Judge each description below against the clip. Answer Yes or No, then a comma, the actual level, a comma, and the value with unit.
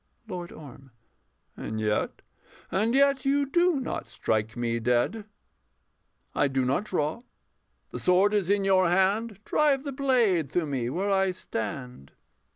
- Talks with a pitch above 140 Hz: Yes, medium, 185 Hz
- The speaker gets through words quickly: No, average, 145 wpm